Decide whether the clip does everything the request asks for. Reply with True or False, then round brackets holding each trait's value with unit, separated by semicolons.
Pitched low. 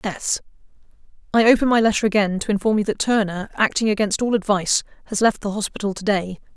False (205 Hz)